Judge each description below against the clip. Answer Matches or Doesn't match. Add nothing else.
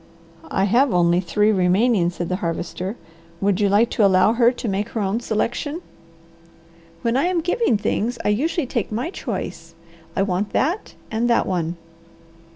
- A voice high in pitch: Matches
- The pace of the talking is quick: Doesn't match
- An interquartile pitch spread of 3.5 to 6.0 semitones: Matches